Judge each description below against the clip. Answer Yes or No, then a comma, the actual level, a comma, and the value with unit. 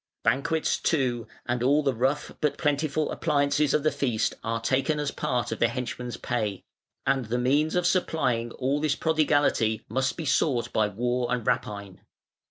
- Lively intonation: No, average, 3.9 semitones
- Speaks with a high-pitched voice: No, low, 130 Hz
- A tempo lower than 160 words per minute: No, average, 170 wpm